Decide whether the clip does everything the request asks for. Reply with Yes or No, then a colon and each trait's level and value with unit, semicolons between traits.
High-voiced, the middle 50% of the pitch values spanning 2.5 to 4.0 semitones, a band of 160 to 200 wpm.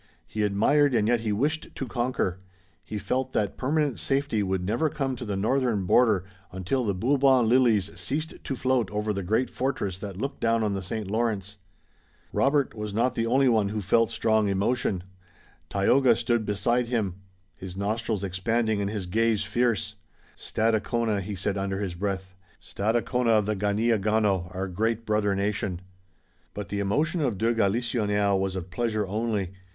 No: low, 110 Hz; average, 3.3 semitones; average, 165 wpm